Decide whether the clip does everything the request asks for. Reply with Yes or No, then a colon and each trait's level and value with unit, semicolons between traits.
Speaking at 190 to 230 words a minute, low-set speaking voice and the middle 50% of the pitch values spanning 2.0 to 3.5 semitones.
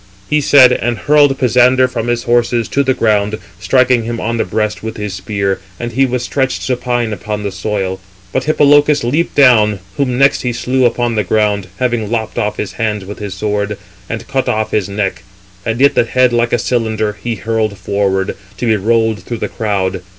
Yes: average, 200 wpm; low, 115 Hz; average, 3.2 semitones